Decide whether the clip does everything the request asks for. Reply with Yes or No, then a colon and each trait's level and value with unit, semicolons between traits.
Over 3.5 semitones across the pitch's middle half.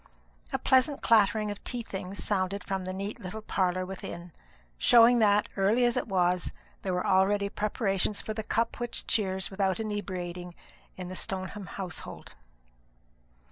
No: narrow, 2.6 semitones